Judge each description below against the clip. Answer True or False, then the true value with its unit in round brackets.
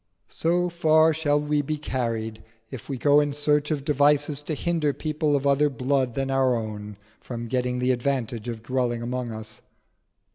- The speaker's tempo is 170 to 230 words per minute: True (175 wpm)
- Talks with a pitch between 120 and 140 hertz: True (135 Hz)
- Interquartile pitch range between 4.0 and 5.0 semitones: False (3.5 semitones)